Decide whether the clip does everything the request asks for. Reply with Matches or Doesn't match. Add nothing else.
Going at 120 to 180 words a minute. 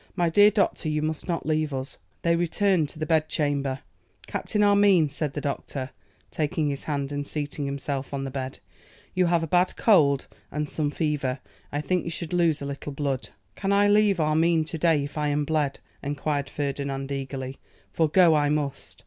Doesn't match